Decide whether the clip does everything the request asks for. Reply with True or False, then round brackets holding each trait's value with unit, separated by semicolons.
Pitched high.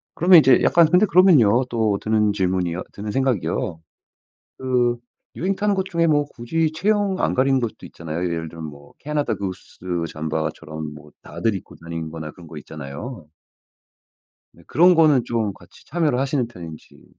False (115 Hz)